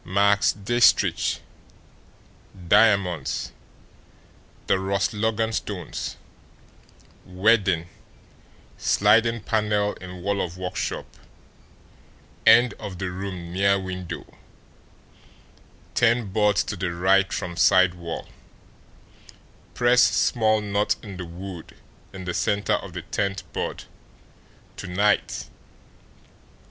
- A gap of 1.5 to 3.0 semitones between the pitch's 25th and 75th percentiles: Yes, narrow, 2.4 semitones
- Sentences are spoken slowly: Yes, slow, 100 wpm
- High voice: No, low, 100 Hz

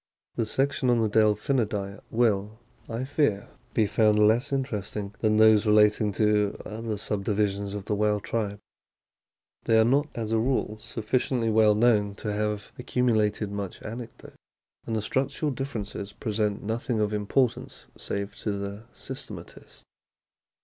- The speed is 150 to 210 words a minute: No, average, 140 wpm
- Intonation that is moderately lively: No, narrow, 1.9 semitones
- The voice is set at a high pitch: No, low, 110 Hz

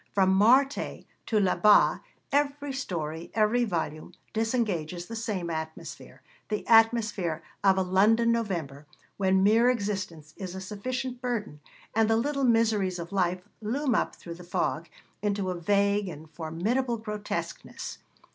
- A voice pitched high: Yes, high, 205 Hz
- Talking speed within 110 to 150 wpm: Yes, average, 140 wpm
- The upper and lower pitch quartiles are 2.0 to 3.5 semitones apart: No, average, 4.6 semitones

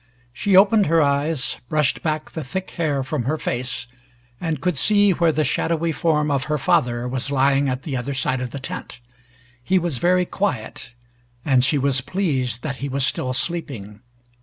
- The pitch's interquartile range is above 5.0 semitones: No, average, 4.2 semitones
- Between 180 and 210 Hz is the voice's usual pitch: No, medium, 140 Hz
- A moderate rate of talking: Yes, average, 185 wpm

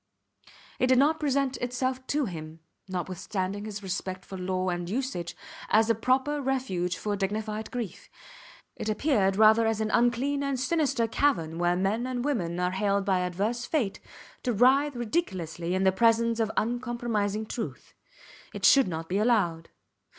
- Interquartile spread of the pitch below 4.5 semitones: No, average, 5.2 semitones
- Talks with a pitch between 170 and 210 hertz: No, high, 220 Hz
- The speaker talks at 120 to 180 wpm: Yes, average, 160 wpm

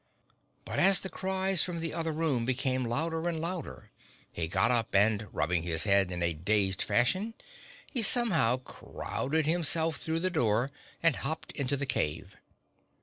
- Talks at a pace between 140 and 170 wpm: Yes, average, 160 wpm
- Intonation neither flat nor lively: No, wide, 8.0 semitones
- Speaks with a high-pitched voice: No, medium, 140 Hz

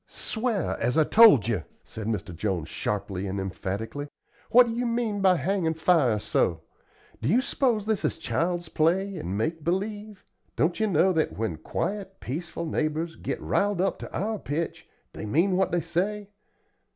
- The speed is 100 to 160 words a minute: No, average, 170 wpm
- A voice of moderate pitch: Yes, medium, 170 Hz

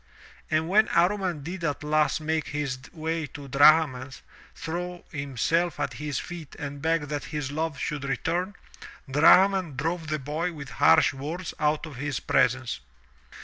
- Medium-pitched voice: Yes, medium, 155 Hz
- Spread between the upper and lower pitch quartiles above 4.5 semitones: No, average, 2.9 semitones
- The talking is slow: No, average, 150 wpm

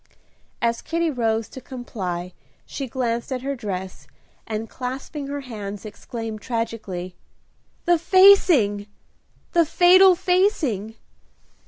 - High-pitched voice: Yes, high, 240 Hz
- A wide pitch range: Yes, wide, 6.6 semitones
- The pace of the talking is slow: Yes, slow, 110 wpm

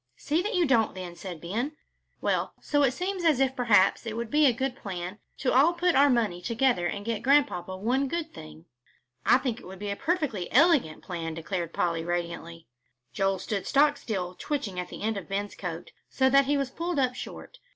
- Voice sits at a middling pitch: No, high, 230 Hz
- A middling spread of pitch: No, wide, 7.4 semitones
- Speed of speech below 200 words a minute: No, fast, 205 wpm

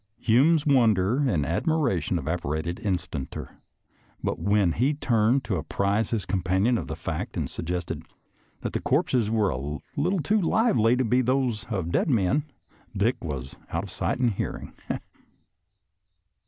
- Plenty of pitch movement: Yes, wide, 6.5 semitones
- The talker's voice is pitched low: Yes, low, 105 Hz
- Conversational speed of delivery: Yes, average, 145 wpm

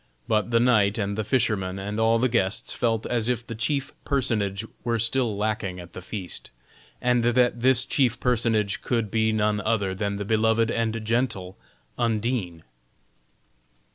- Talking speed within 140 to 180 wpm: Yes, average, 160 wpm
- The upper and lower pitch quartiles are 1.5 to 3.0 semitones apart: Yes, average, 2.7 semitones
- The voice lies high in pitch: No, low, 110 Hz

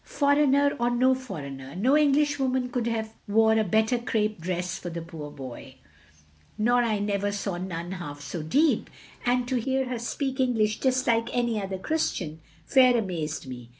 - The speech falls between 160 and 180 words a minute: Yes, average, 170 wpm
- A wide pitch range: Yes, wide, 6.2 semitones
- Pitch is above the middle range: Yes, high, 220 Hz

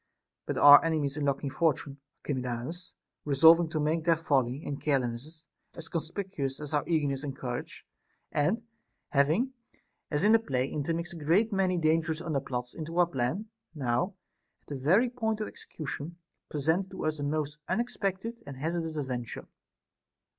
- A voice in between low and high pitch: Yes, medium, 155 Hz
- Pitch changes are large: No, average, 3.7 semitones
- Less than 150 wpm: No, average, 155 wpm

